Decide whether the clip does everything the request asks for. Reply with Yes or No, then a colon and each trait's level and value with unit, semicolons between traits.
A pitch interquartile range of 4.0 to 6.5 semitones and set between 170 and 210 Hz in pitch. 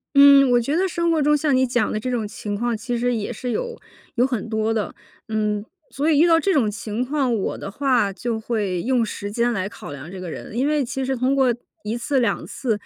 No: average, 4.3 semitones; high, 240 Hz